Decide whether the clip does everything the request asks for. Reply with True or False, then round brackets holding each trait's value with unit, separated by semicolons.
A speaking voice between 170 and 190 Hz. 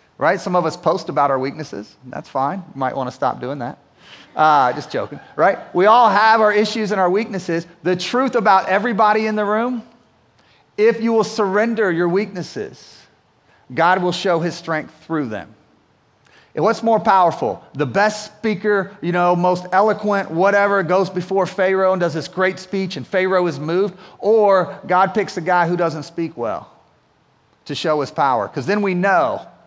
True (185 Hz)